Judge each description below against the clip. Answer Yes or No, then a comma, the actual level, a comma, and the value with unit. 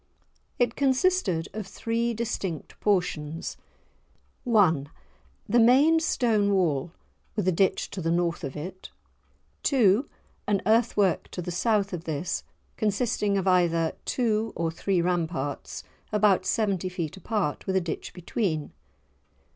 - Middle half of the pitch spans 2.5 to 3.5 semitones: No, average, 4.7 semitones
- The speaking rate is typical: No, slow, 130 wpm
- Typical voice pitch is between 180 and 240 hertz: Yes, high, 190 Hz